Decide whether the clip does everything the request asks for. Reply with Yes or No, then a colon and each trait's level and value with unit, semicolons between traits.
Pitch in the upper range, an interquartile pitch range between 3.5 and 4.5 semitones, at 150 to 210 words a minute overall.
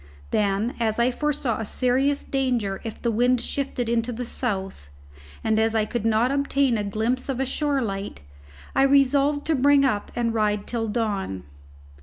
Yes: high, 235 Hz; average, 3.8 semitones; average, 175 wpm